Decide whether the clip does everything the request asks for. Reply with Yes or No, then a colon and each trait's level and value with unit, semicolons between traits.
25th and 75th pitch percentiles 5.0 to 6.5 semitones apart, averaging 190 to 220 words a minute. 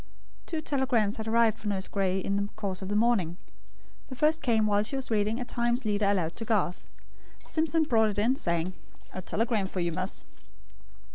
No: average, 3.6 semitones; average, 195 wpm